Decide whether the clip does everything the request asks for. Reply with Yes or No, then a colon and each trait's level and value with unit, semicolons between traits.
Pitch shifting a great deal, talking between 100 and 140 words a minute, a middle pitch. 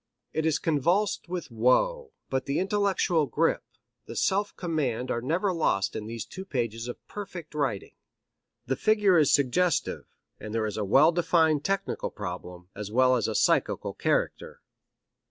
No: wide, 7.8 semitones; average, 155 wpm; medium, 150 Hz